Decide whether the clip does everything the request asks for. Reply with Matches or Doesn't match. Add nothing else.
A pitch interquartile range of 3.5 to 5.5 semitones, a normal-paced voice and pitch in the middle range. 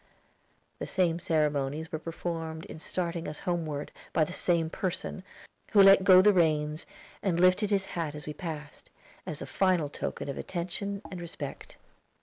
Doesn't match